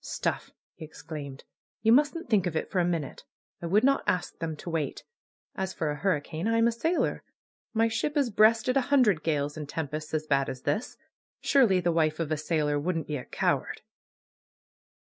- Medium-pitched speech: Yes, medium, 170 Hz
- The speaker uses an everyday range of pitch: No, wide, 6.7 semitones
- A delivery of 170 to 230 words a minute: Yes, average, 190 wpm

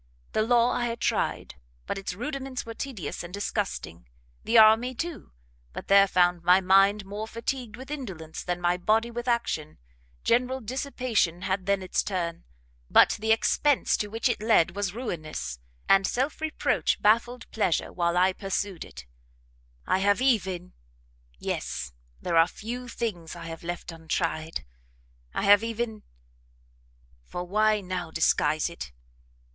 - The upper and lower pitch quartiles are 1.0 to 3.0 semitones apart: No, average, 5.1 semitones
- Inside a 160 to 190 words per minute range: No, average, 150 wpm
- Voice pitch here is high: Yes, high, 200 Hz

